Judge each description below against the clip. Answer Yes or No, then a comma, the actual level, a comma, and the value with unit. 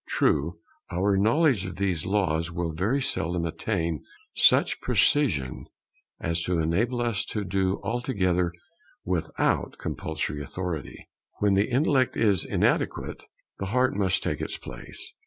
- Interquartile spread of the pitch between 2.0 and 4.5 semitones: No, average, 5.0 semitones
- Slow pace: Yes, slow, 130 wpm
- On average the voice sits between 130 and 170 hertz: No, very low, 95 Hz